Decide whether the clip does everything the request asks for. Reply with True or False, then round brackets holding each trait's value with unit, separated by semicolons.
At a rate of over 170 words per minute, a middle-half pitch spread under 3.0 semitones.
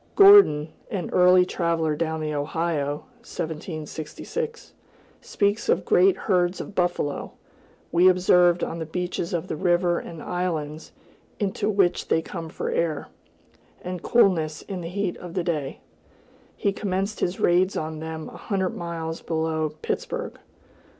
False (140 wpm; 2.6 semitones)